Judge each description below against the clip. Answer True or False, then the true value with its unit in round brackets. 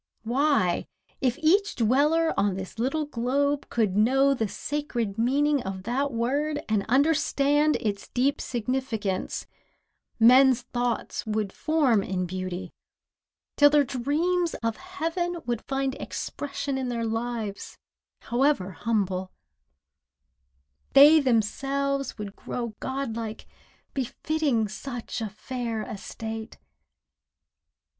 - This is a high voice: True (250 Hz)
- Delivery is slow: True (105 wpm)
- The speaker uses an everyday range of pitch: True (4.5 semitones)